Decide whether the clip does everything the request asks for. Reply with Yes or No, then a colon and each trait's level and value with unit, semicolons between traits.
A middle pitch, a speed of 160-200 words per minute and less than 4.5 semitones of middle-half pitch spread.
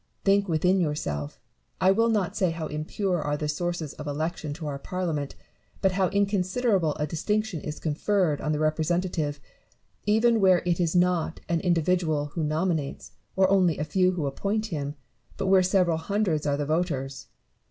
Yes: medium, 170 Hz; average, 175 wpm; average, 3.9 semitones